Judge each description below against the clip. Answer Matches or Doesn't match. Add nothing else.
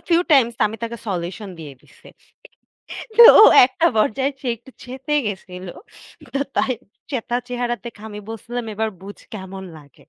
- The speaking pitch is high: Matches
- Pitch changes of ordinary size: Matches